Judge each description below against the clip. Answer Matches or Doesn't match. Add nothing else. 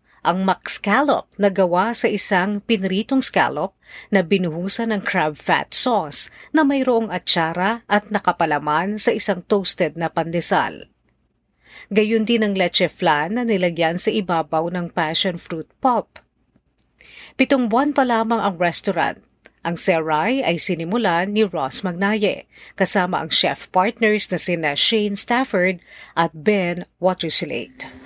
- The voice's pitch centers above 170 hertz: Matches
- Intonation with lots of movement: Doesn't match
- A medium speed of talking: Matches